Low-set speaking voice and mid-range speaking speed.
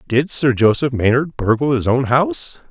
Yes: low, 125 Hz; average, 180 wpm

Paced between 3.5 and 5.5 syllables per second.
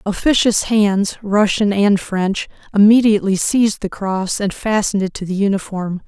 Yes: 4.8 syllables/s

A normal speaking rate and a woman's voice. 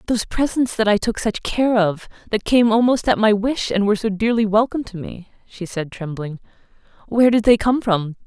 No: fast, 210 wpm; female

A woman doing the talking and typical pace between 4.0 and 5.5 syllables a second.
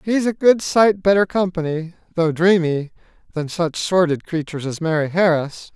No: male; 4.6 syllables/s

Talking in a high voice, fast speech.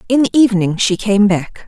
Yes: high, 210 Hz; fast, 215 wpm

